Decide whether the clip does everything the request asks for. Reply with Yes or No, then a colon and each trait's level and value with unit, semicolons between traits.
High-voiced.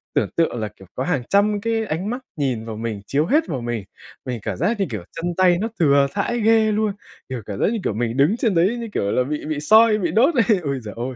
No: medium, 165 Hz